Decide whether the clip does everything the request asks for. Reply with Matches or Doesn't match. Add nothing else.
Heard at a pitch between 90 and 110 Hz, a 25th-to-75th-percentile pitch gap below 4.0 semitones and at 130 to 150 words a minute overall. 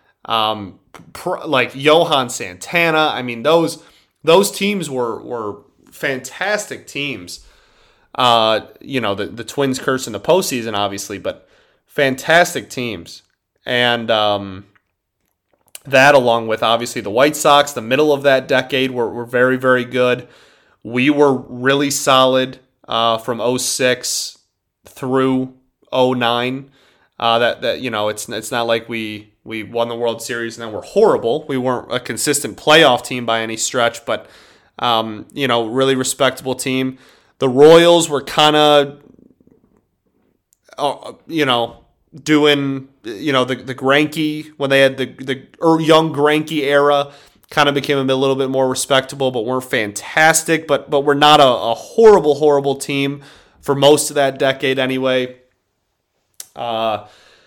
Doesn't match